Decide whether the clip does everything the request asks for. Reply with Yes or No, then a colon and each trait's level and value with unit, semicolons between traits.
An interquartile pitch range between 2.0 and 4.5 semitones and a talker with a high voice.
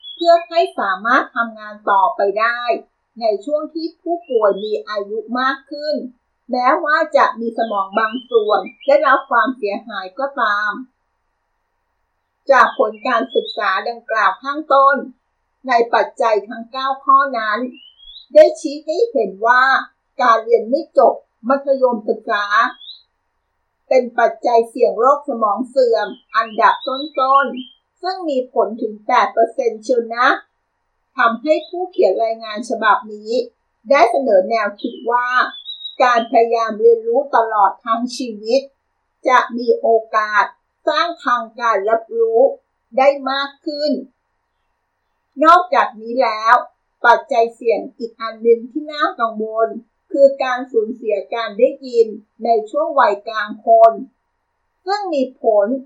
Yes: average, 4.1 semitones; very high, 250 Hz